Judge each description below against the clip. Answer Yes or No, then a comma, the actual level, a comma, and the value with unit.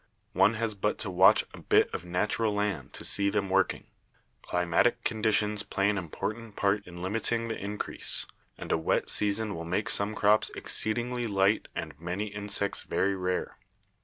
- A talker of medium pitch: No, low, 100 Hz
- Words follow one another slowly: No, average, 165 wpm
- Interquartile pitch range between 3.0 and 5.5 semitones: No, narrow, 2.4 semitones